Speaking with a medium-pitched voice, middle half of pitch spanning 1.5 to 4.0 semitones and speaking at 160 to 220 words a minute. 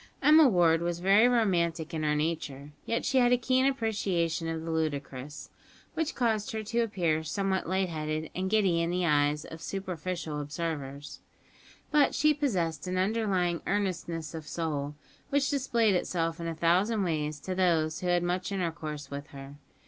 No: medium, 175 Hz; average, 4.5 semitones; average, 170 wpm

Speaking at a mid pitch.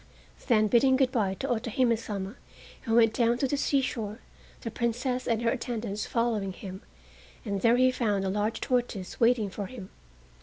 No: high, 230 Hz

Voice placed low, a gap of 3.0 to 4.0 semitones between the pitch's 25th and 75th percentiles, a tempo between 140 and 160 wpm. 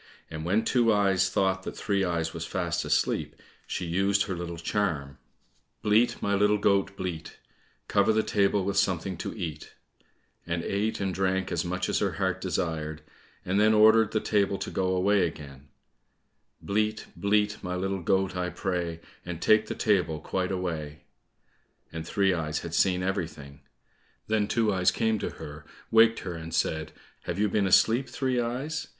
No: very low, 95 Hz; average, 3.5 semitones; average, 170 wpm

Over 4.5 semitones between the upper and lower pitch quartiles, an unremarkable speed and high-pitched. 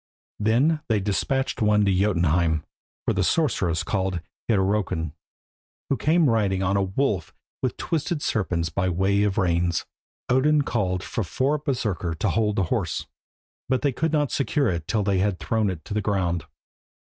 No: wide, 5.5 semitones; average, 165 wpm; low, 100 Hz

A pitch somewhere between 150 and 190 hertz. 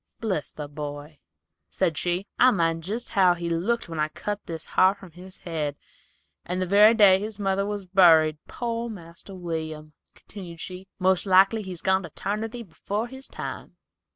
Yes: medium, 185 Hz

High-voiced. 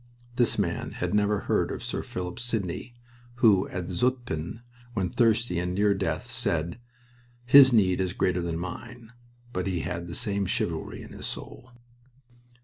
No: low, 100 Hz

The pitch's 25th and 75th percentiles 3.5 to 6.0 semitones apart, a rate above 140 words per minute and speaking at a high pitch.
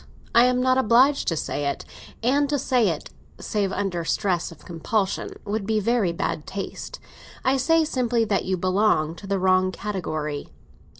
Yes: average, 5.3 semitones; average, 170 wpm; high, 205 Hz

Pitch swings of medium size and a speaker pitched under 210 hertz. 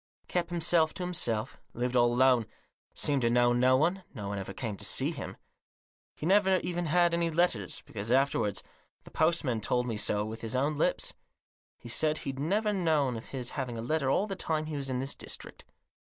No: wide, 5.8 semitones; low, 135 Hz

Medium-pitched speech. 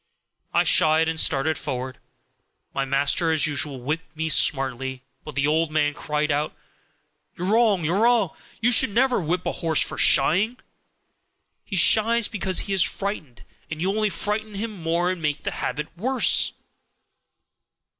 Yes: medium, 165 Hz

